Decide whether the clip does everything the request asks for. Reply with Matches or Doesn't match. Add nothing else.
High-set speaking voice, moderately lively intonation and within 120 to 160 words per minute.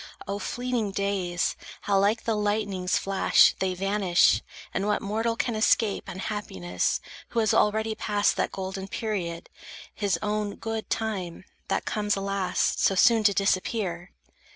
Doesn't match